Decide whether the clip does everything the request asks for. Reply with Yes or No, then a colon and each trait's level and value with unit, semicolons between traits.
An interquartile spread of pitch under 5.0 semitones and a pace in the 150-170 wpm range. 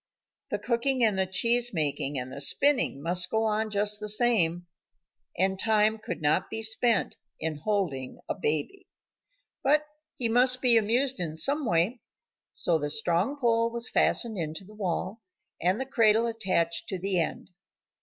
No: wide, 5.4 semitones; average, 165 wpm